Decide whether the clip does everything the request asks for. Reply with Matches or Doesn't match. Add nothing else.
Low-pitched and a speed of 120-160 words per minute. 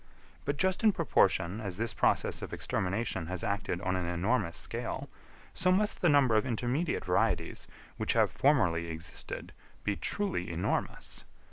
Matches